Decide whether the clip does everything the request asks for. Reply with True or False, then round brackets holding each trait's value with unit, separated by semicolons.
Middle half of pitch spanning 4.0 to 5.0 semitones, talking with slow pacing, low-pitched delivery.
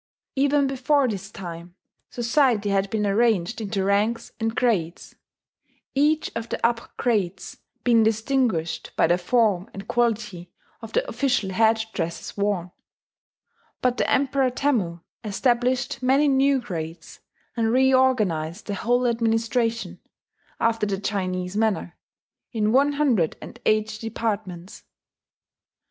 False (4.3 semitones; 125 wpm; 225 Hz)